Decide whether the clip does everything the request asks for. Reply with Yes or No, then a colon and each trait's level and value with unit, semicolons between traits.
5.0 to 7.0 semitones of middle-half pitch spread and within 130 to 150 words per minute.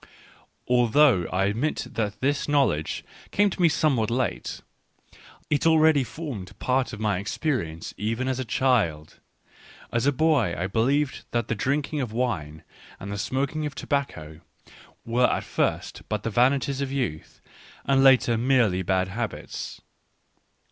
Yes: wide, 5.5 semitones; average, 145 wpm